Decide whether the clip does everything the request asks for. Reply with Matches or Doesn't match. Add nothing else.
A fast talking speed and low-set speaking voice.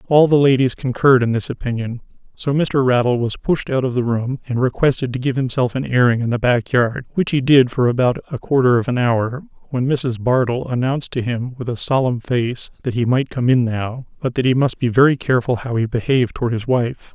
Matches